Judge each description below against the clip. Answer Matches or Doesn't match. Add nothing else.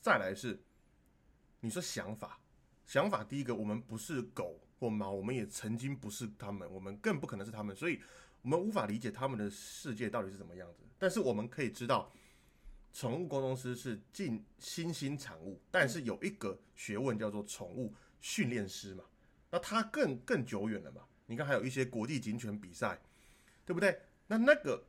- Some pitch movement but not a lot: Matches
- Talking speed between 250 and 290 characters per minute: Matches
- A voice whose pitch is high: Doesn't match